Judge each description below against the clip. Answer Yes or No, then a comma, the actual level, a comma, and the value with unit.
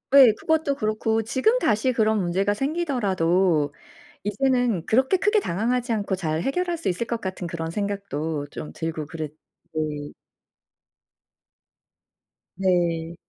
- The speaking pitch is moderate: No, high, 200 Hz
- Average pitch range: No, wide, 7.0 semitones